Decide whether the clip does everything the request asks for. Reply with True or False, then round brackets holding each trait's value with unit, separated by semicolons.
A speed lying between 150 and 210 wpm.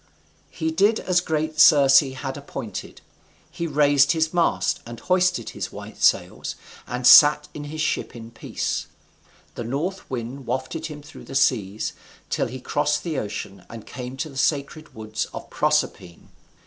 True (160 wpm)